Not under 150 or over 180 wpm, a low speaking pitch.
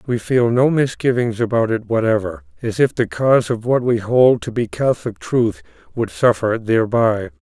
Yes: average, 175 wpm; low, 120 Hz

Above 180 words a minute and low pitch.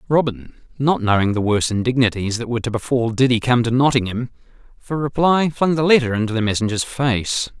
Yes: average, 190 wpm; low, 120 Hz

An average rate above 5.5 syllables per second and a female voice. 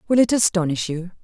Yes: 6.3 syllables/s; female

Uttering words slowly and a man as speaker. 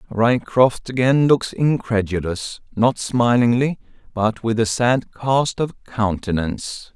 Yes: slow, 110 wpm; male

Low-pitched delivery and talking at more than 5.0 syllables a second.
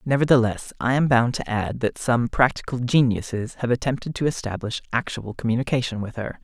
Yes: low, 120 Hz; 5.5 syllables/s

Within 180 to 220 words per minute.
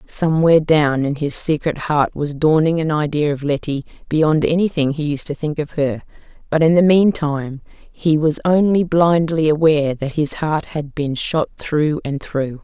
Yes: average, 185 wpm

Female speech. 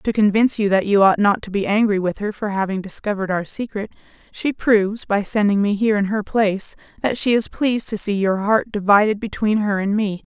Yes: female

